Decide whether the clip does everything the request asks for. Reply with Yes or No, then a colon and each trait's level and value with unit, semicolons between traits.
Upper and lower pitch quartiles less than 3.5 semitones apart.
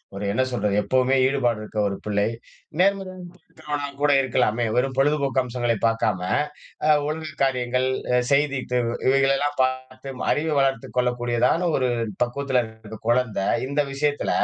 Yes: average, 2.9 semitones